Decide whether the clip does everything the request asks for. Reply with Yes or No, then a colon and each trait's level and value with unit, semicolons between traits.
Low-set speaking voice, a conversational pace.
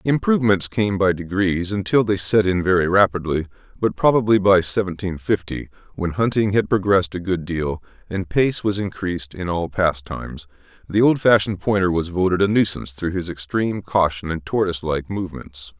Yes: very low, 95 Hz; average, 165 wpm